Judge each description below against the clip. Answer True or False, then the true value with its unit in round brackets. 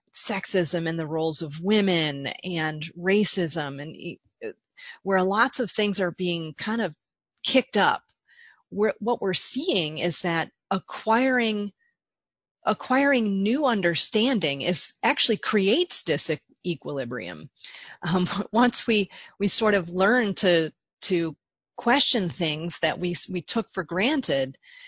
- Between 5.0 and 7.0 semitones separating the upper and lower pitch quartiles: True (5.3 semitones)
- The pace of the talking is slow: True (125 wpm)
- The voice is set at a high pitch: True (195 Hz)